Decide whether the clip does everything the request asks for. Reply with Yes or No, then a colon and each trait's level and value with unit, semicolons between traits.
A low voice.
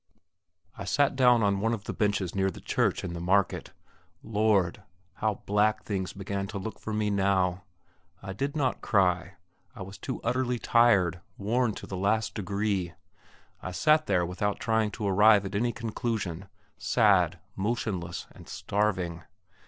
Yes: low, 100 Hz